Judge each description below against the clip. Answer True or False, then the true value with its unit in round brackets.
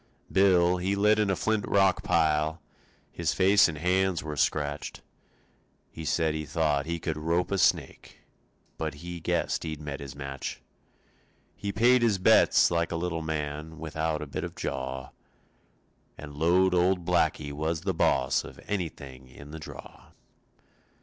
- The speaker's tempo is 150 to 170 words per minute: True (155 wpm)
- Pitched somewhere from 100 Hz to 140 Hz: False (80 Hz)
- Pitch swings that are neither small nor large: True (3.5 semitones)